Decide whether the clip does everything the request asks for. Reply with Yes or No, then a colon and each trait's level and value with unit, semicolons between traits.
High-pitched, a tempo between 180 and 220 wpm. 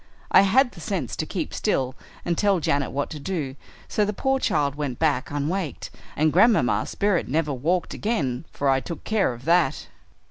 No: medium, 155 Hz; average, 185 wpm